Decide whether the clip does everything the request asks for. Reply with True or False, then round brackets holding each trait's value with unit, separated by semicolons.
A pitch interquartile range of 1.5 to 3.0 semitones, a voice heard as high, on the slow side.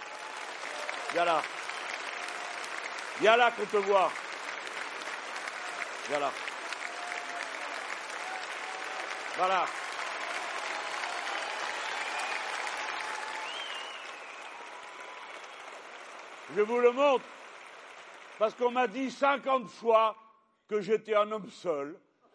True (2.7 semitones; 220 Hz; 65 wpm)